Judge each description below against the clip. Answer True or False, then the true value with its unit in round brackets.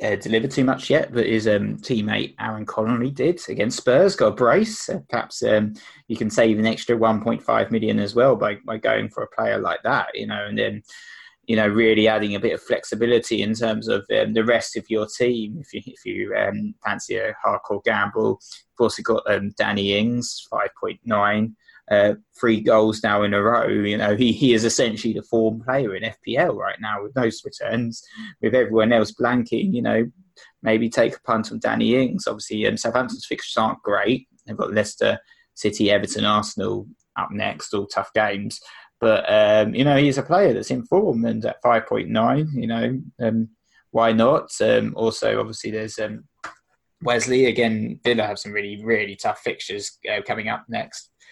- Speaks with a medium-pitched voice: False (115 Hz)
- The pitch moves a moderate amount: False (2.3 semitones)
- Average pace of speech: True (195 wpm)